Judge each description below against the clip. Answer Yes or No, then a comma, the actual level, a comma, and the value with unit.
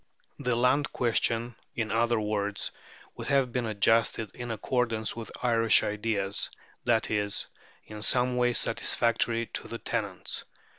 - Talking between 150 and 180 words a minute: No, slow, 135 wpm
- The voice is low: Yes, low, 115 Hz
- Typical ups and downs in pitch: No, narrow, 2.1 semitones